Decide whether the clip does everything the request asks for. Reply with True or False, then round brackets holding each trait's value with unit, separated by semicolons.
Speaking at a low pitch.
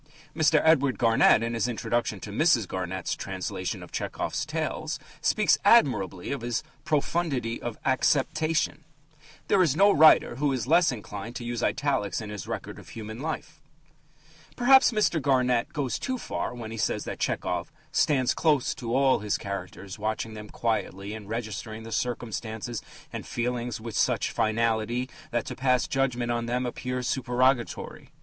True (120 Hz)